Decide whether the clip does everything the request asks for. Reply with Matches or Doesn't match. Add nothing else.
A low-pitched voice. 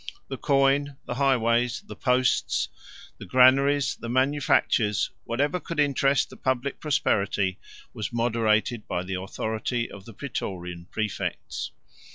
Matches